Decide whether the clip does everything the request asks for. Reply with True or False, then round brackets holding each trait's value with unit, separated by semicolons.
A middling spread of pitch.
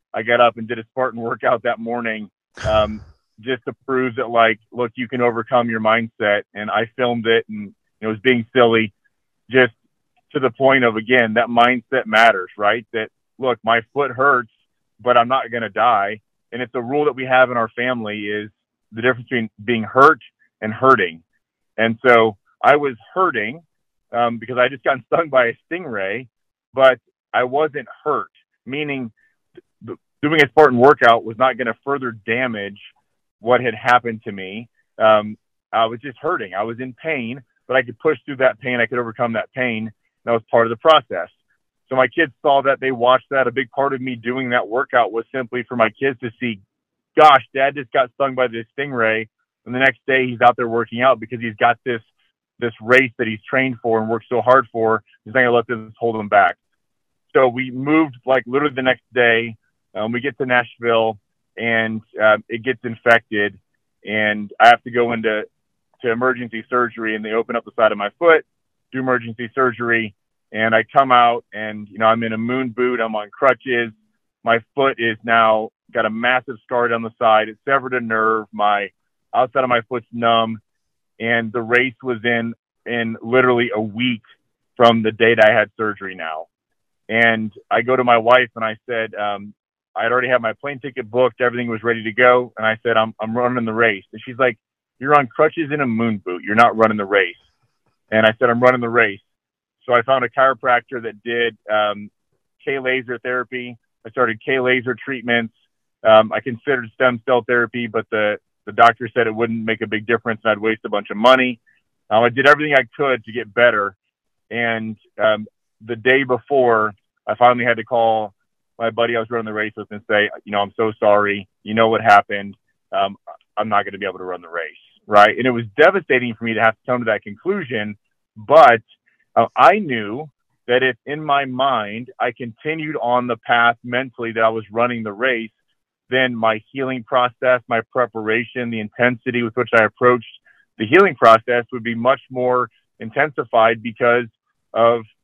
False (2.3 semitones)